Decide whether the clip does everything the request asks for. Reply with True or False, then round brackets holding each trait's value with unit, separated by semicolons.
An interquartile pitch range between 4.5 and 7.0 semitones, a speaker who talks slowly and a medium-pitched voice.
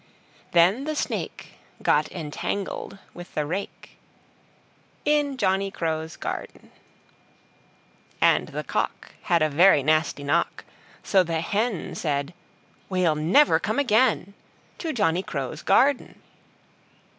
True (5.4 semitones; 110 wpm; 180 Hz)